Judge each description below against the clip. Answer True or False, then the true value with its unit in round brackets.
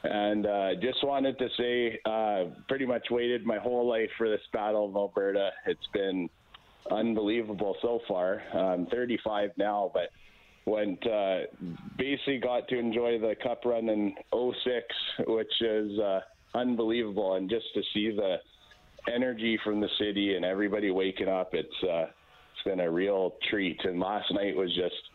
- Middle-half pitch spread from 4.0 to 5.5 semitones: False (3.4 semitones)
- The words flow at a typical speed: True (160 wpm)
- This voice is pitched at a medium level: False (110 Hz)